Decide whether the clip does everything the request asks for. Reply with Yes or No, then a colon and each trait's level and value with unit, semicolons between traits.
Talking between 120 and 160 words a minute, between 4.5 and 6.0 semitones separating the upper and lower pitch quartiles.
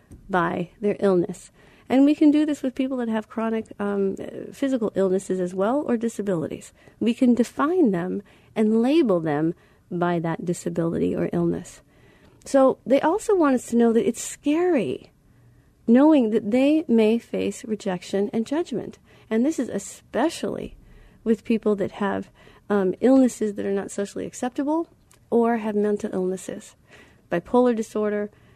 Yes: average, 150 wpm; average, 5.1 semitones